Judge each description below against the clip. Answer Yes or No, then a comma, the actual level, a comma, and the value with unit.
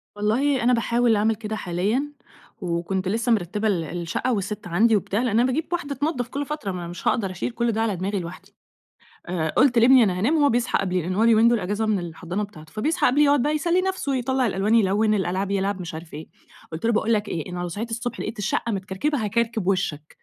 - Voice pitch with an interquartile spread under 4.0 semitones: No, average, 4.5 semitones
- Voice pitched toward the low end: No, high, 215 Hz